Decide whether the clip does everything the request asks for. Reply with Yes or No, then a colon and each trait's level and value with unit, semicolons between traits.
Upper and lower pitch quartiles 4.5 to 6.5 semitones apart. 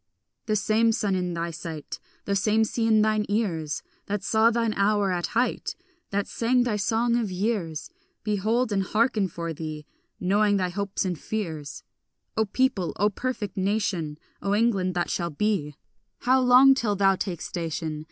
No: average, 3.8 semitones